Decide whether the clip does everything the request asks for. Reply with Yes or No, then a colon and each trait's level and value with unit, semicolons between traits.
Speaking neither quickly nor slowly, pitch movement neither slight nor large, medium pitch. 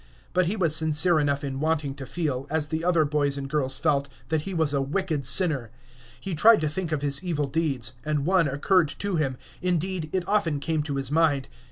No: fast, 215 wpm; average, 3.3 semitones; medium, 155 Hz